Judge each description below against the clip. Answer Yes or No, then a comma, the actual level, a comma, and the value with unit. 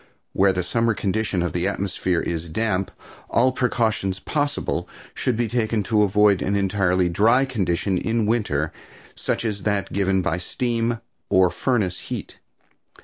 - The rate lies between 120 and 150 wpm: Yes, average, 145 wpm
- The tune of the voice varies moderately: Yes, average, 3.8 semitones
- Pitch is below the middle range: Yes, low, 100 Hz